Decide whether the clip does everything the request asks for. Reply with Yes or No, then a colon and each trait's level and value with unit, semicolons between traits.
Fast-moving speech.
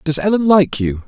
Yes: fast, 225 wpm